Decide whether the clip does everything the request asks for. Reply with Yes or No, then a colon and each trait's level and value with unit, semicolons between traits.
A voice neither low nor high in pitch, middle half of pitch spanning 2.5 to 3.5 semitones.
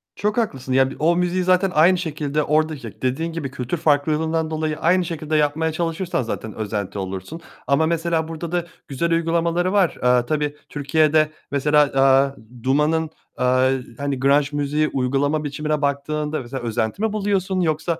Yes: medium, 155 Hz; average, 3.2 semitones